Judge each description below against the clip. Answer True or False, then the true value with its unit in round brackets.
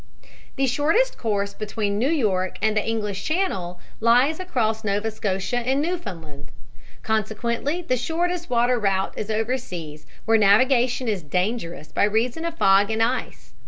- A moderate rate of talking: True (150 wpm)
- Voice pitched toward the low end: False (225 Hz)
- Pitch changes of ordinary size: True (4.4 semitones)